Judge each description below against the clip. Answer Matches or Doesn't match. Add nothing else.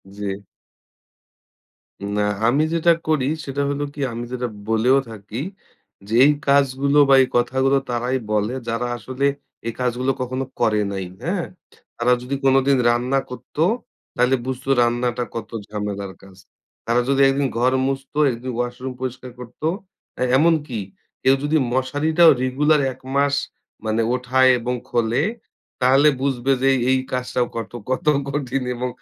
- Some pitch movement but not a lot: Doesn't match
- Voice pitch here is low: Matches